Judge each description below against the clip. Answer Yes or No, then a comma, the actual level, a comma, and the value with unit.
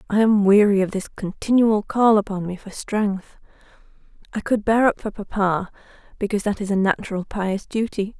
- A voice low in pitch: No, high, 205 Hz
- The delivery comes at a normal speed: Yes, average, 175 wpm